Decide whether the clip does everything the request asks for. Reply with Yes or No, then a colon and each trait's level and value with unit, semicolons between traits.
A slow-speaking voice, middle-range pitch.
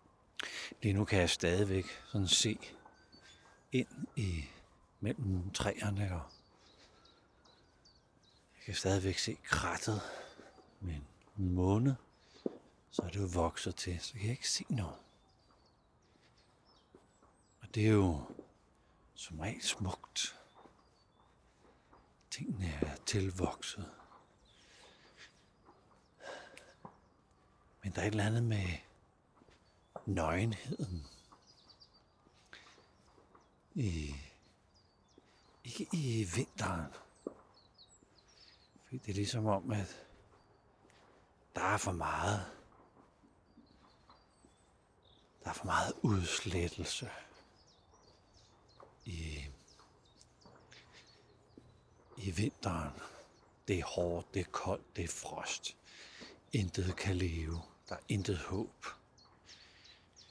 No: slow, 90 wpm; very low, 95 Hz